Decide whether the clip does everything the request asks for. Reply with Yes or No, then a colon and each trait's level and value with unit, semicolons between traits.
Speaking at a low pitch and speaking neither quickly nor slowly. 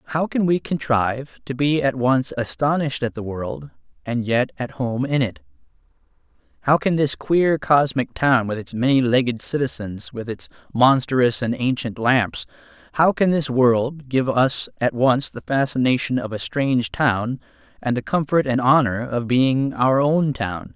Yes: low, 130 Hz; average, 170 wpm